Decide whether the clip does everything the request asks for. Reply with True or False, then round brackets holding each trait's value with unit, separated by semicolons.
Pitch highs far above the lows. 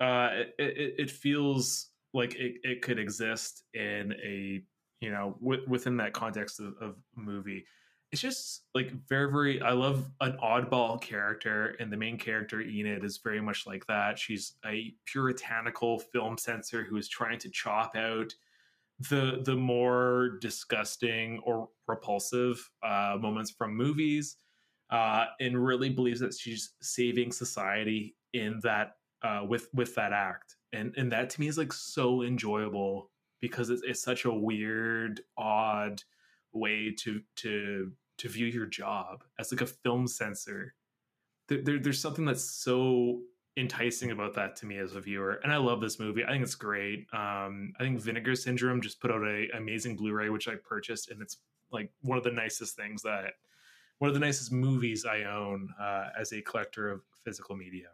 False (2.9 semitones)